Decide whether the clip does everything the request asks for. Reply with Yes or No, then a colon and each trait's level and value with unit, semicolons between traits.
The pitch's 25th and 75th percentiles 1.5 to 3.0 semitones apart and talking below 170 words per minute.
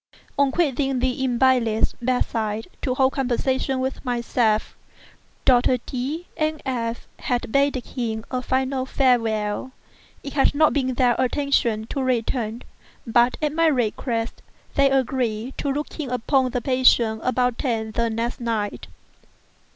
Yes: narrow, 2.5 semitones; average, 140 wpm